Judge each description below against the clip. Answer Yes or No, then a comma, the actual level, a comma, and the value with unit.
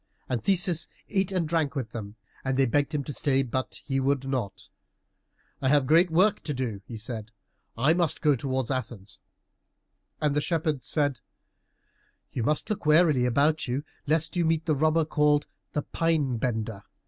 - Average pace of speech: Yes, average, 175 wpm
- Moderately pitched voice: Yes, medium, 145 Hz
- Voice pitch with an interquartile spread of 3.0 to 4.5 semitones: Yes, average, 3.9 semitones